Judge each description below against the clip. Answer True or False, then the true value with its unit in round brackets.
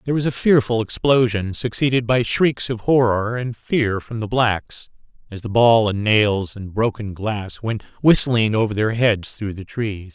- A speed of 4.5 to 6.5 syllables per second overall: False (4.3 syllables/s)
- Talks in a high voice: False (115 Hz)